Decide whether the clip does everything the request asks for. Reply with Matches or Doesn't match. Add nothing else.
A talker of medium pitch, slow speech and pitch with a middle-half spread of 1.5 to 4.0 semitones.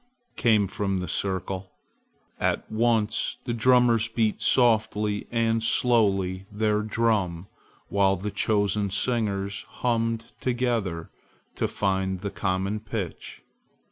Doesn't match